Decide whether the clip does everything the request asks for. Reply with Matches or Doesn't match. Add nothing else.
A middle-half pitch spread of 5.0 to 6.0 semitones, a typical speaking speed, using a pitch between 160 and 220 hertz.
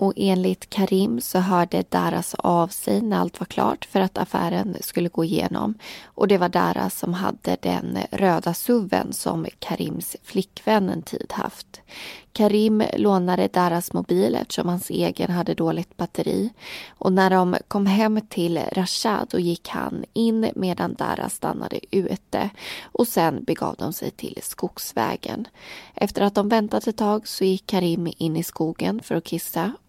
Doesn't match